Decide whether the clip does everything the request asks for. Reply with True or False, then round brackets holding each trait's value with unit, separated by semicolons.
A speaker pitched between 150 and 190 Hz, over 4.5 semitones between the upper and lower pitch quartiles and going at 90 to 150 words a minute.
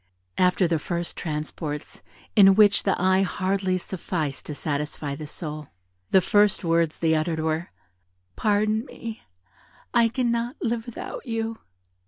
True (185 Hz; 5.2 semitones; 135 wpm)